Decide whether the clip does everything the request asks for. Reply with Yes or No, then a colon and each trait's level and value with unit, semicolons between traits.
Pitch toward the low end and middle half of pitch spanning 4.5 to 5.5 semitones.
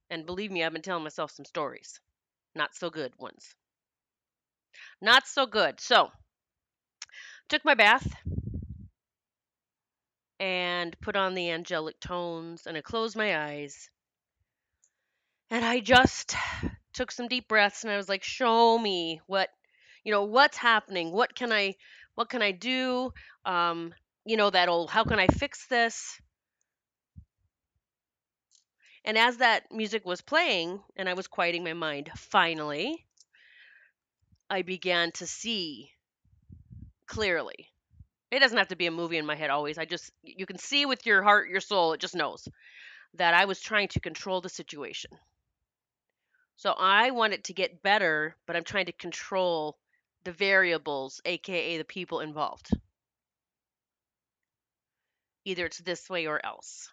No: high, 190 Hz; average, 4.8 semitones